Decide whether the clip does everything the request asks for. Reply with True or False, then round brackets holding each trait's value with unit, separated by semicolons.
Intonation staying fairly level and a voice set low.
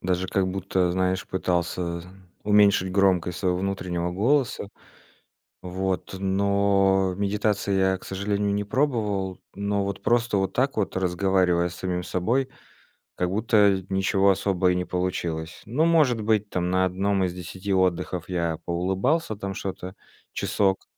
True (1.9 semitones; 95 Hz)